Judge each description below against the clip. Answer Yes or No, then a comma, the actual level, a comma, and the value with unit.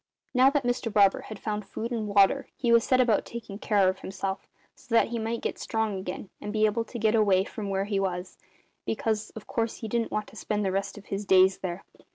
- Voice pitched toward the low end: No, high, 210 Hz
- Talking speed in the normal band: No, fast, 230 wpm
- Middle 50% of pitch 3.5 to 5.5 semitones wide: No, average, 2.7 semitones